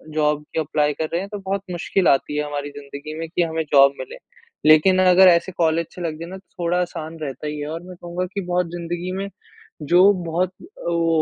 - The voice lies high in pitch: No, medium, 170 Hz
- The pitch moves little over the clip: No, average, 3.0 semitones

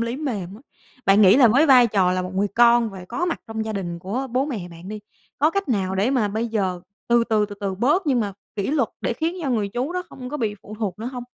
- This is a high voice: Yes, high, 225 Hz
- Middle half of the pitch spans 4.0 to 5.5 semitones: Yes, average, 4.6 semitones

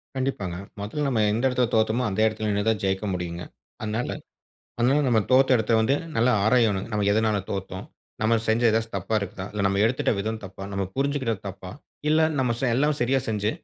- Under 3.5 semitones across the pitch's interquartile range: No, average, 3.8 semitones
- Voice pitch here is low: Yes, low, 110 Hz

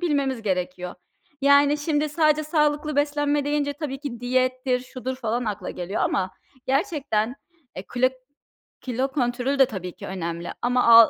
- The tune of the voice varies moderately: Yes, average, 4.1 semitones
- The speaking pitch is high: Yes, very high, 260 Hz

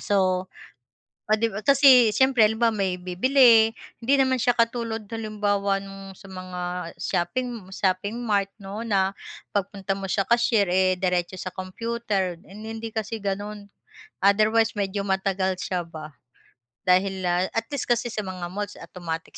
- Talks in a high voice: Yes, high, 200 Hz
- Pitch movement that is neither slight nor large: Yes, average, 3.3 semitones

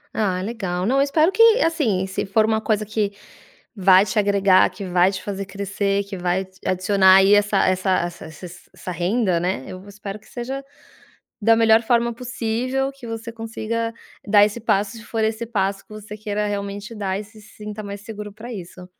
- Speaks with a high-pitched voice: Yes, high, 205 Hz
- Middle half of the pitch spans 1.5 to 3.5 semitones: Yes, average, 2.8 semitones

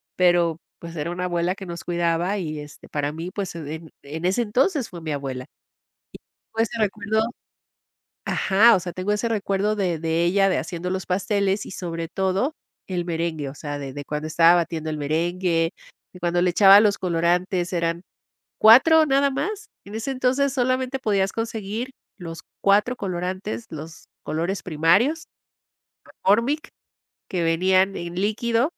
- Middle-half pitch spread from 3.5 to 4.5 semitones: Yes, average, 4.2 semitones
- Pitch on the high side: No, medium, 180 Hz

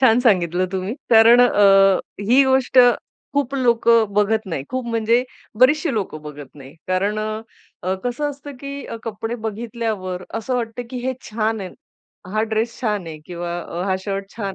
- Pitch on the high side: Yes, high, 220 Hz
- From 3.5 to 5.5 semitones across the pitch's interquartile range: Yes, average, 4.0 semitones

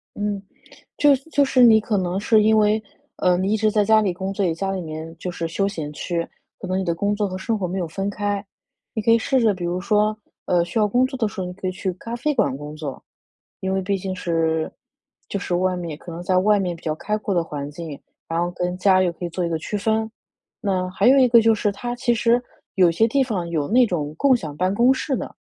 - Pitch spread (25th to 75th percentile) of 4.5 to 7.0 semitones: No, average, 3.8 semitones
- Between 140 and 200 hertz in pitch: Yes, high, 190 Hz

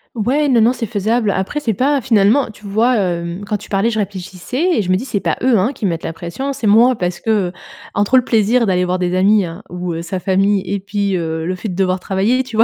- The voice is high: Yes, high, 205 Hz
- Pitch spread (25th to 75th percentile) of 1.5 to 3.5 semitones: No, average, 4.1 semitones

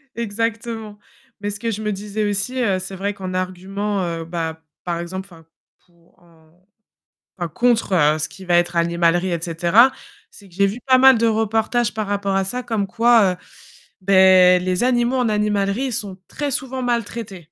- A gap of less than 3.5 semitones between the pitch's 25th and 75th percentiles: No, average, 4.0 semitones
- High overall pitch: Yes, high, 200 Hz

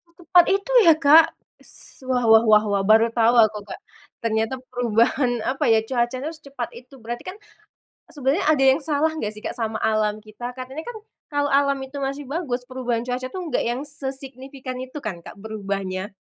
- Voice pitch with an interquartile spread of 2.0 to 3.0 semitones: No, average, 4.1 semitones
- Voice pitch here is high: Yes, very high, 255 Hz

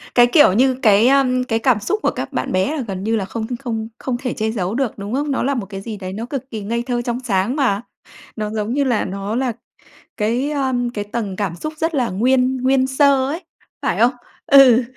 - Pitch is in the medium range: No, high, 240 Hz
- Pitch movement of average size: Yes, average, 4.0 semitones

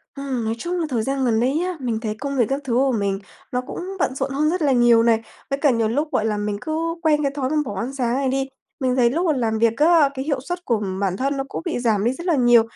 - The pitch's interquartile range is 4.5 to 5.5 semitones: No, average, 4.0 semitones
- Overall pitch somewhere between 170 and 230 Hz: No, very high, 260 Hz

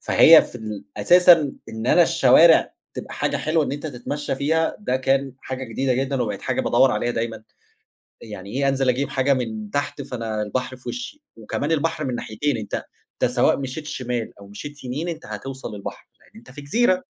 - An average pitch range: Yes, average, 4.2 semitones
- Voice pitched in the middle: No, low, 130 Hz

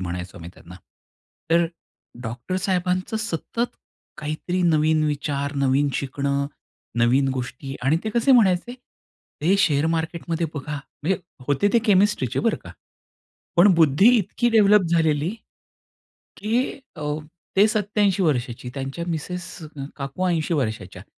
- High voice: No, medium, 160 Hz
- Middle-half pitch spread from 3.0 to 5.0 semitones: No, wide, 5.5 semitones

